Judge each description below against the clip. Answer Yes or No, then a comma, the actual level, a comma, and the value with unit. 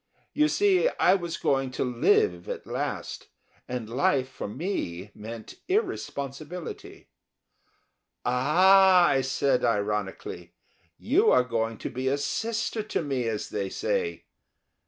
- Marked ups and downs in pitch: Yes, wide, 8.8 semitones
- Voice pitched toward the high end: No, low, 135 Hz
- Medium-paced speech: No, slow, 125 wpm